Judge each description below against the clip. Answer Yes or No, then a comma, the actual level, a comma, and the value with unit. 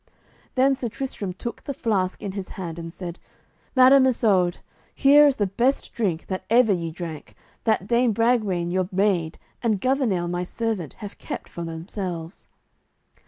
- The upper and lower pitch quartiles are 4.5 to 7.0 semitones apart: Yes, average, 5.3 semitones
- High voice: Yes, high, 200 Hz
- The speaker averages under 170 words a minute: Yes, average, 160 wpm